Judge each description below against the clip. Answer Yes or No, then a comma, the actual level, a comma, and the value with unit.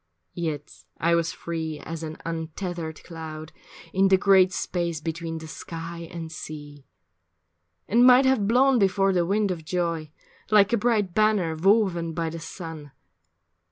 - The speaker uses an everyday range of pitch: Yes, average, 3.3 semitones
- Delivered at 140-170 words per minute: Yes, average, 150 wpm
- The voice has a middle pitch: Yes, medium, 170 Hz